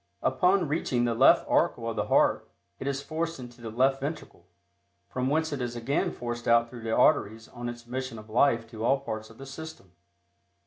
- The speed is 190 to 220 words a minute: Yes, fast, 205 wpm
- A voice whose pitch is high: No, low, 125 Hz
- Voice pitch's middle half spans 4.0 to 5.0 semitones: No, average, 3.1 semitones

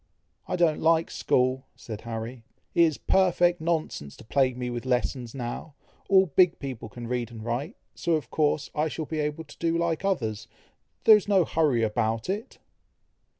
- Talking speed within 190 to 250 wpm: No, average, 180 wpm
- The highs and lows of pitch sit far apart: Yes, wide, 5.8 semitones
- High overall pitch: No, medium, 145 Hz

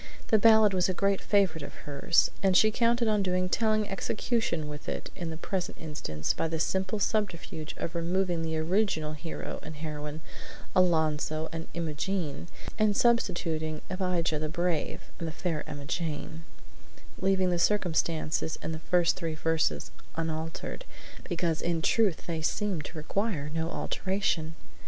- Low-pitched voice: No, medium, 170 Hz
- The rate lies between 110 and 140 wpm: No, average, 150 wpm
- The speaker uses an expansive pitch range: No, average, 3.4 semitones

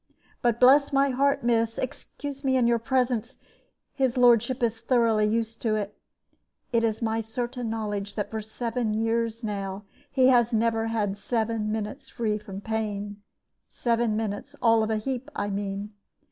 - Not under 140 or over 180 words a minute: Yes, average, 160 wpm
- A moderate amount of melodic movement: No, narrow, 2.3 semitones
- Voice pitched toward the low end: No, high, 225 Hz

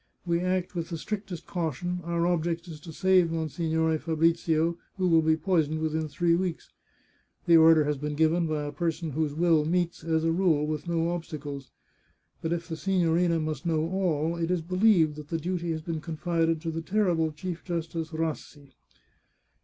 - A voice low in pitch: No, medium, 165 Hz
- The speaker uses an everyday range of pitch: No, narrow, 1.7 semitones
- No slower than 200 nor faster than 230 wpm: No, average, 180 wpm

